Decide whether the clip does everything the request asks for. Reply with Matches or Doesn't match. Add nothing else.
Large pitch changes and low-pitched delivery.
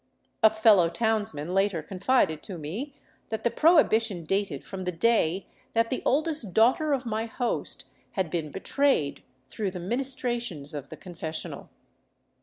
Doesn't match